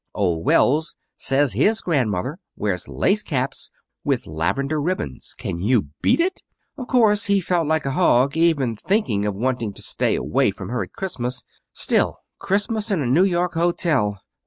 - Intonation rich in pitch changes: Yes, wide, 8.0 semitones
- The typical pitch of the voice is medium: Yes, medium, 145 Hz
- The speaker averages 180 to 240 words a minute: No, average, 165 wpm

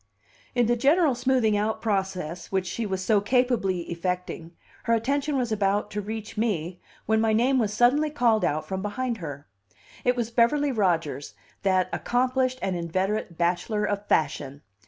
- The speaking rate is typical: Yes, average, 160 wpm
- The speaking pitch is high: Yes, high, 210 Hz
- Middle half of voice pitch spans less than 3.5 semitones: No, average, 4.8 semitones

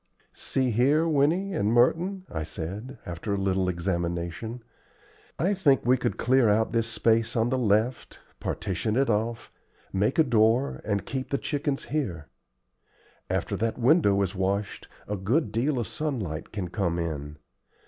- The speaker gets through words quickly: No, average, 155 wpm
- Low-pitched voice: Yes, low, 115 Hz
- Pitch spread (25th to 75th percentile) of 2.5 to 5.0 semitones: No, wide, 5.6 semitones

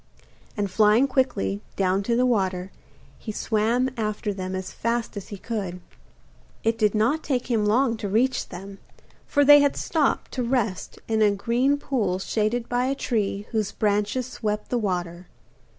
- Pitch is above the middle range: Yes, high, 215 Hz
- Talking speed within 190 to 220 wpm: No, average, 165 wpm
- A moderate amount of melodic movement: Yes, average, 3.7 semitones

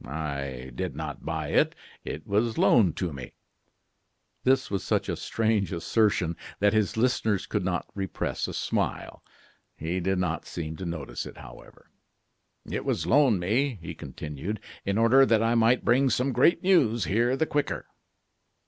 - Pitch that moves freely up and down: Yes, wide, 5.7 semitones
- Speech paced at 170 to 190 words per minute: No, average, 160 wpm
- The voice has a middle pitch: No, low, 105 Hz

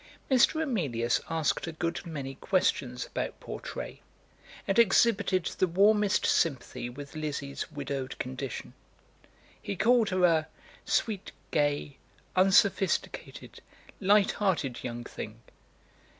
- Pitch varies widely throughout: Yes, wide, 6.2 semitones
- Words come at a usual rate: No, slow, 105 wpm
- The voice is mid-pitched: Yes, medium, 165 Hz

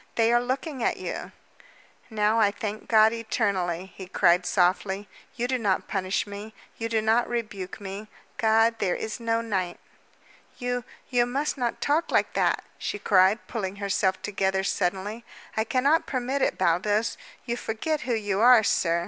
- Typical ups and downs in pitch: Yes, average, 3.7 semitones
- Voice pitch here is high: Yes, high, 220 Hz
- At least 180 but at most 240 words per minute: No, average, 165 wpm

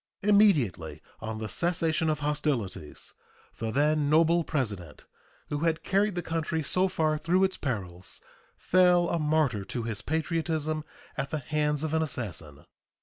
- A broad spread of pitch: Yes, wide, 6.0 semitones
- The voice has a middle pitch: Yes, medium, 155 Hz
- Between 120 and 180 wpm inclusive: Yes, average, 145 wpm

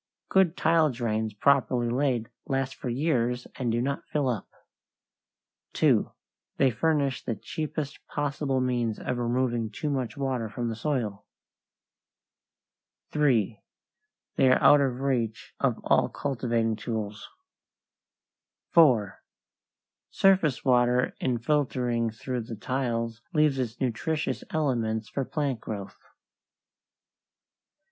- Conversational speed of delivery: No, slow, 115 wpm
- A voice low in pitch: Yes, low, 125 Hz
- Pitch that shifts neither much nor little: Yes, average, 3.4 semitones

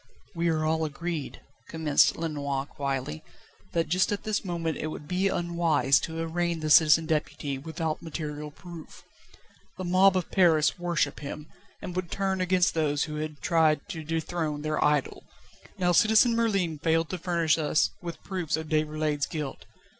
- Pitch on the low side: No, medium, 160 Hz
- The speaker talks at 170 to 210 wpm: No, average, 160 wpm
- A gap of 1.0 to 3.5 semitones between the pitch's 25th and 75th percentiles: Yes, narrow, 2.5 semitones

